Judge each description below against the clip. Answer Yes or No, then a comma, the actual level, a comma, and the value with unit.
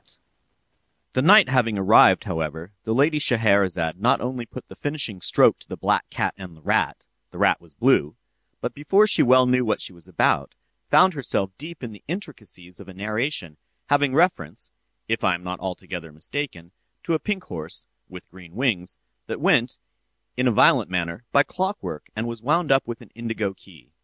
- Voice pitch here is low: Yes, low, 110 Hz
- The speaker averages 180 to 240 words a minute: Yes, average, 185 wpm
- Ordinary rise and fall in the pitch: No, wide, 7.5 semitones